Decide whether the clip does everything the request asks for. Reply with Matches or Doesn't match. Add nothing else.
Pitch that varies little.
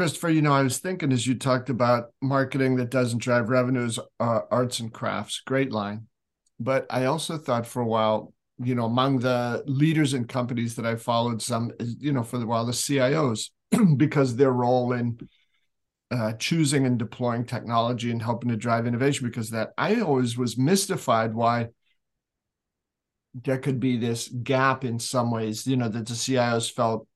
Matches